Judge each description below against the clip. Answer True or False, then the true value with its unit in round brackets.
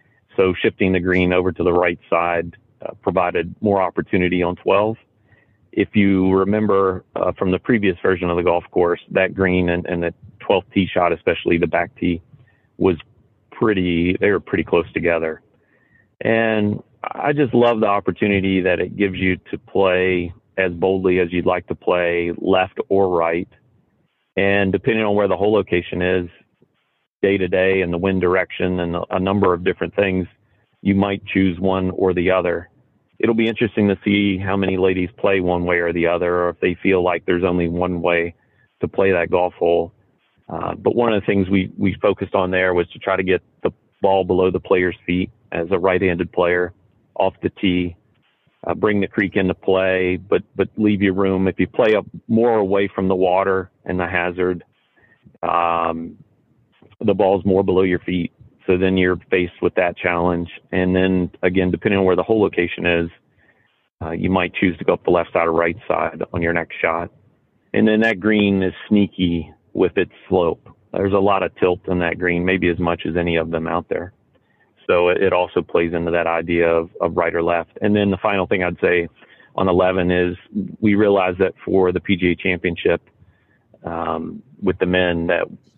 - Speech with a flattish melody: True (2.2 semitones)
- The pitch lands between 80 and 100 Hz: True (95 Hz)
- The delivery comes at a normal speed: True (190 wpm)